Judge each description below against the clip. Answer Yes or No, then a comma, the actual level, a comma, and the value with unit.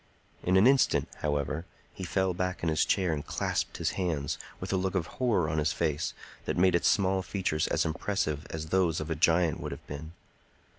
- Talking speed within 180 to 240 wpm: Yes, fast, 205 wpm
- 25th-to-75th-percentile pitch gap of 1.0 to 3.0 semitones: No, average, 3.4 semitones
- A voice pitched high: No, very low, 85 Hz